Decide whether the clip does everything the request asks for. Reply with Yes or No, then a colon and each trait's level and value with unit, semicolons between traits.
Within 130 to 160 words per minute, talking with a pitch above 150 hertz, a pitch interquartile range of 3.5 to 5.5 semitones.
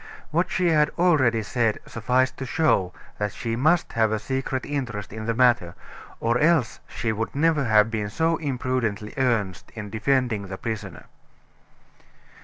No: average, 155 wpm; low, 115 Hz; average, 4.2 semitones